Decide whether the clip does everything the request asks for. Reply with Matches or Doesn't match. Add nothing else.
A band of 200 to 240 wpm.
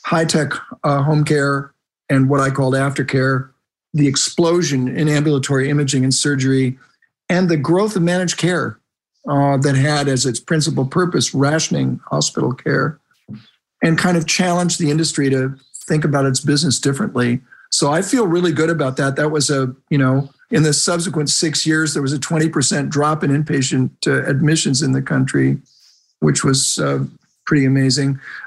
Doesn't match